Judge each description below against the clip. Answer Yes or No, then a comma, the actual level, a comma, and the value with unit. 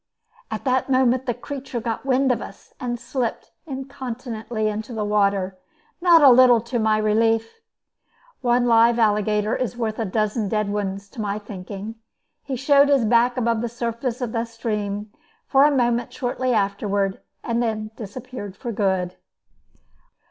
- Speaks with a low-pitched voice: No, high, 230 Hz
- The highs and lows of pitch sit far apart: No, average, 3.0 semitones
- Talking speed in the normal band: Yes, average, 155 wpm